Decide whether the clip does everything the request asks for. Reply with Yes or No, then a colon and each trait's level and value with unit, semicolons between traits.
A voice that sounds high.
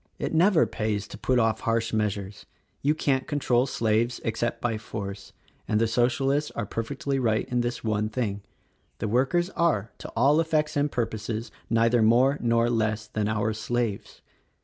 No: low, 115 Hz